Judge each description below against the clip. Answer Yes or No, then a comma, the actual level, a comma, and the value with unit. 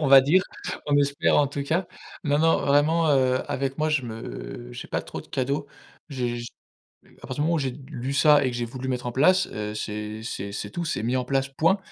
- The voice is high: No, low, 135 Hz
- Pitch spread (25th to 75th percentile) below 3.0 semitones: No, average, 3.3 semitones